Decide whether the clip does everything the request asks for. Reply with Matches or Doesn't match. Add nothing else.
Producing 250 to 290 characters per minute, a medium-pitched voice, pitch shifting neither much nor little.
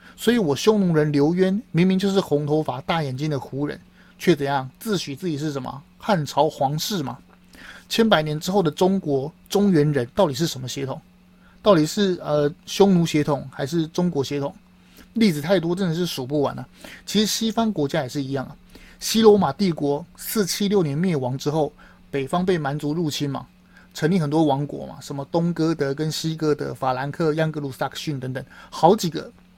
Matches